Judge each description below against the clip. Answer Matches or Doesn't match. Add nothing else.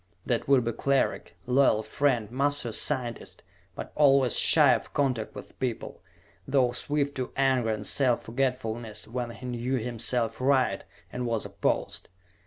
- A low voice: Matches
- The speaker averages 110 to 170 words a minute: Matches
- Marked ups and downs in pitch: Doesn't match